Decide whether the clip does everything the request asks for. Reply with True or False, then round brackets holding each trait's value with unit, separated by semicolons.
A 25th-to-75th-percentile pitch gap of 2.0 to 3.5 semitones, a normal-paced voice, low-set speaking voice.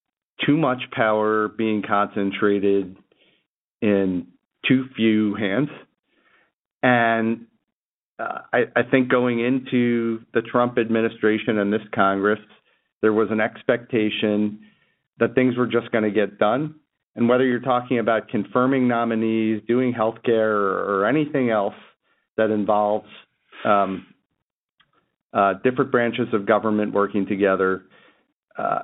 False (2.6 semitones; 125 wpm; 110 Hz)